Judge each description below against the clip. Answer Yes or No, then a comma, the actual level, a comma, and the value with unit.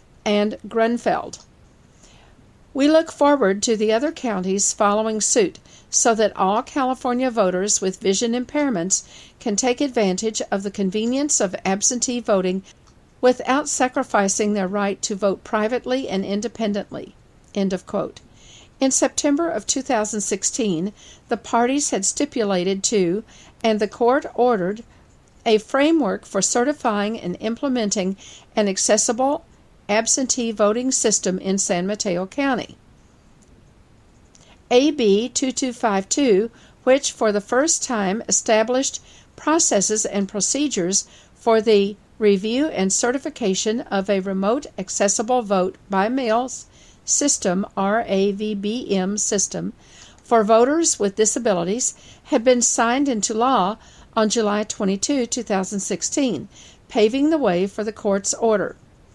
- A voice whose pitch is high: Yes, high, 220 Hz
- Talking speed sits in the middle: No, slow, 115 wpm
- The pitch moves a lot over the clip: No, average, 4.0 semitones